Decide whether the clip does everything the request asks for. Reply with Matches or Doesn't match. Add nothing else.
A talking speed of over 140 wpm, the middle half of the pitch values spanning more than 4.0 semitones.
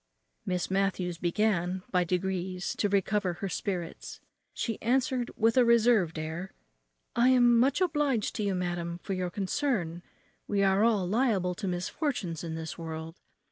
Matches